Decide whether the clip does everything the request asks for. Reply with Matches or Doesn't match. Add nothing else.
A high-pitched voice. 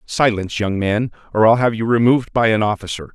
Doesn't match